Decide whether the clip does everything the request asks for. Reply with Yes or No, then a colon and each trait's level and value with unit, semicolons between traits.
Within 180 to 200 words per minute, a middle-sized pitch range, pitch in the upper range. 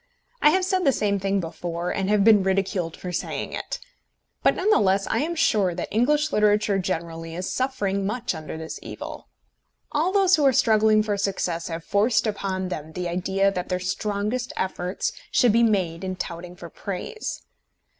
Yes: average, 185 wpm; average, 3.8 semitones; high, 195 Hz